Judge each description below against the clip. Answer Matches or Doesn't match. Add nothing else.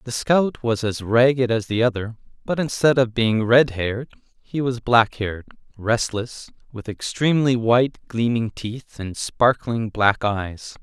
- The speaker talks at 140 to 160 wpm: Matches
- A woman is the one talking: Doesn't match